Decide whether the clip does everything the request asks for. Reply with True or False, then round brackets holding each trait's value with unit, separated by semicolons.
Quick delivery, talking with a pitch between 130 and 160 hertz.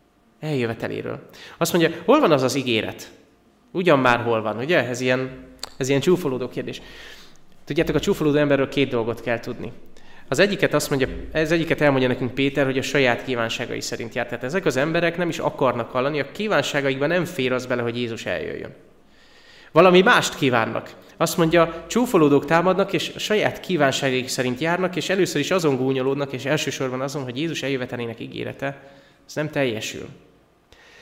True (170 wpm; 140 Hz)